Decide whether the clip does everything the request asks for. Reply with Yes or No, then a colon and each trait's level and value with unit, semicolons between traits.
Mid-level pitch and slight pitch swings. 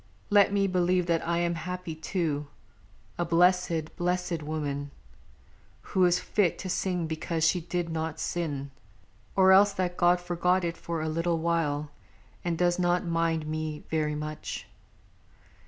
Yes: medium, 170 Hz; narrow, 2.1 semitones